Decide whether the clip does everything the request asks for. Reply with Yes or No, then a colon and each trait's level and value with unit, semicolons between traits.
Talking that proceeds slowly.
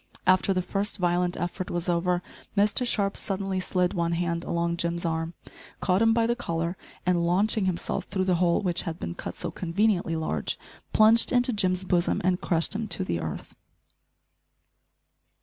No: average, 170 wpm